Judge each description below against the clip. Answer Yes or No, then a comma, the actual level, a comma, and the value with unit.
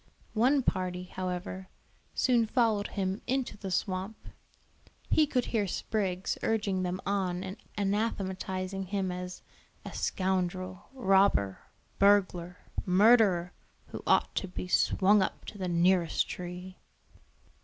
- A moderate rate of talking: No, slow, 120 wpm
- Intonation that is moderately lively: No, narrow, 2.2 semitones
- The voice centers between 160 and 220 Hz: Yes, high, 190 Hz